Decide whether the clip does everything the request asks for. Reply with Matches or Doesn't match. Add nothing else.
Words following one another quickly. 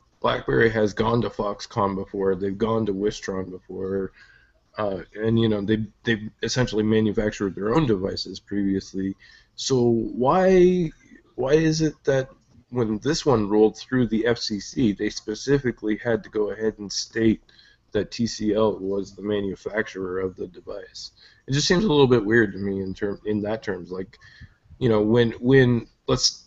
Doesn't match